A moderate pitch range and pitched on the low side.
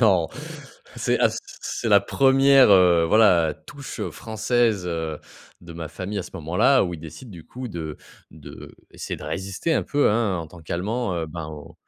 No: wide, 5.8 semitones; very low, 95 Hz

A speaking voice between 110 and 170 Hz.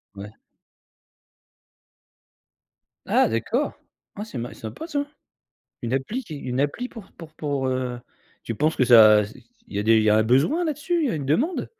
Yes: low, 135 Hz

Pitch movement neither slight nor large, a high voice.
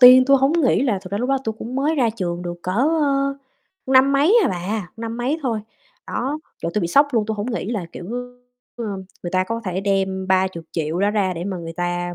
No: wide, 6.0 semitones; high, 210 Hz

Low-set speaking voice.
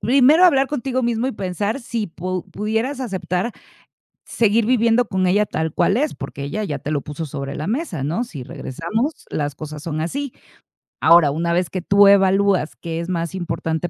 No: high, 190 Hz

